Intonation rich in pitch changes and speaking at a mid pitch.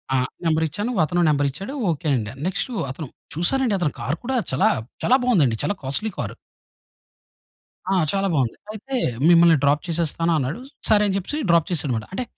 Yes: wide, 6.0 semitones; medium, 170 Hz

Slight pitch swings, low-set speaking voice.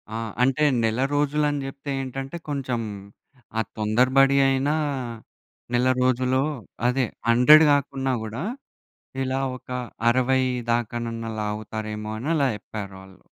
No: average, 3.1 semitones; low, 130 Hz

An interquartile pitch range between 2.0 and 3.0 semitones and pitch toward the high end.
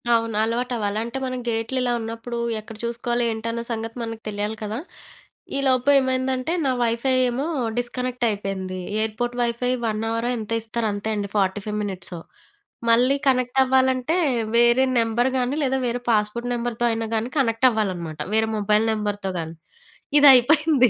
Yes: average, 2.7 semitones; high, 230 Hz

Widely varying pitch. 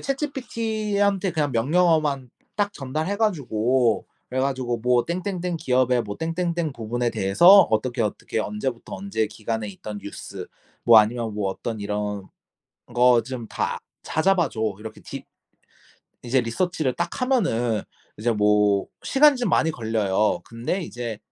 Yes: wide, 7.8 semitones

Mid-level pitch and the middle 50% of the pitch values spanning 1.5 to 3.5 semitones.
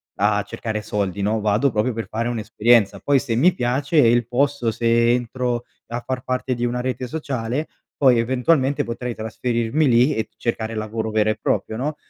No: low, 120 Hz; narrow, 2.5 semitones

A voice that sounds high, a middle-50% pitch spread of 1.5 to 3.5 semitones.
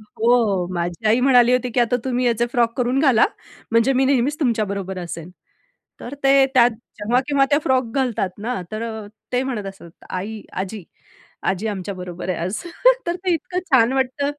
No: high, 235 Hz; average, 4.7 semitones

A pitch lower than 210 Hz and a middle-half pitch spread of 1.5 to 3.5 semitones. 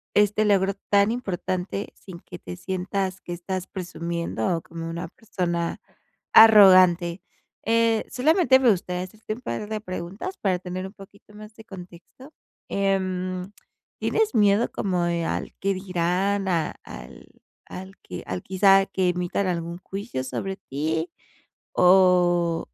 Yes: medium, 185 Hz; narrow, 2.5 semitones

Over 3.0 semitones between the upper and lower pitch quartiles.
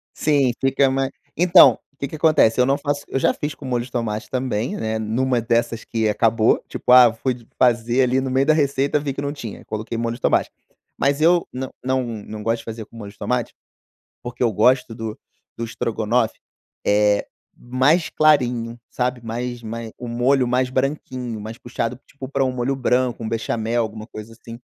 No: average, 2.7 semitones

